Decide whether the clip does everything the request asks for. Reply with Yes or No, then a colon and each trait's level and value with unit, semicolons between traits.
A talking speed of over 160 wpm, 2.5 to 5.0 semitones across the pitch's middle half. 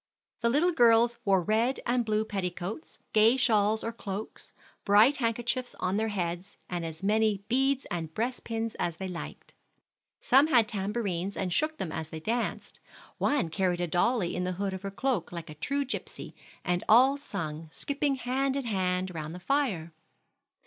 No: average, 170 wpm; wide, 5.4 semitones